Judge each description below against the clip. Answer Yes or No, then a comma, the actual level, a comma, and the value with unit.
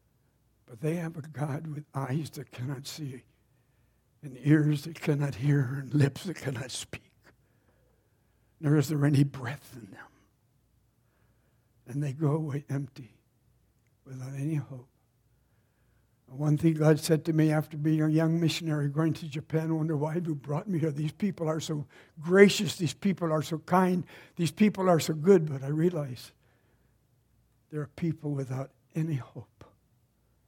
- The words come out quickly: No, average, 160 wpm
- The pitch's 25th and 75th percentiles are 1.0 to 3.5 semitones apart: No, average, 4.0 semitones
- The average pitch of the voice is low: No, medium, 145 Hz